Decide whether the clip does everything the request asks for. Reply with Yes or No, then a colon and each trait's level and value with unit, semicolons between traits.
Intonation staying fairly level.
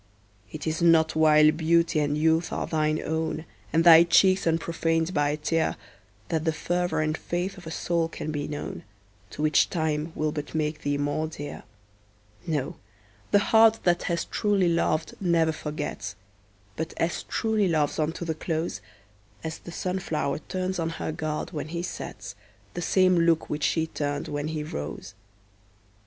Yes: narrow, 1.9 semitones